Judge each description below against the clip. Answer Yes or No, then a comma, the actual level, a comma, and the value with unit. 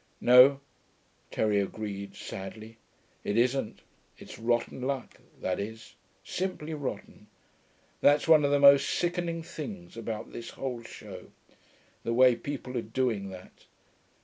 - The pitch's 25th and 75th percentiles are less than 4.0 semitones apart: No, average, 4.6 semitones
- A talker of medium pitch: No, low, 125 Hz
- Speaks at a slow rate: Yes, slow, 125 wpm